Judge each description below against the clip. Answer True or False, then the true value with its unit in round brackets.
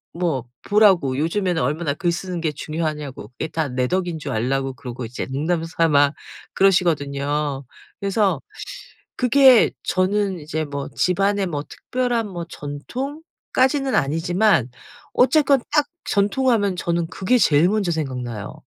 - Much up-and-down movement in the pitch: True (6.0 semitones)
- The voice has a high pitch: False (170 Hz)